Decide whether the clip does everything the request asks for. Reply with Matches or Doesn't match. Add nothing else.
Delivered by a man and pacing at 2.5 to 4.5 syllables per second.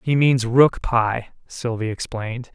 Matches